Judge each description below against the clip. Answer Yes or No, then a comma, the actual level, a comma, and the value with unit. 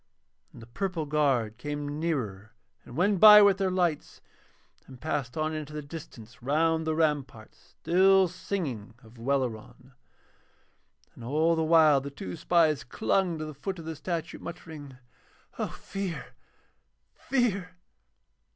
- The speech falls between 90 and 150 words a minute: Yes, average, 140 wpm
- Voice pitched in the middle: Yes, medium, 155 Hz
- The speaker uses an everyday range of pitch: Yes, average, 4.5 semitones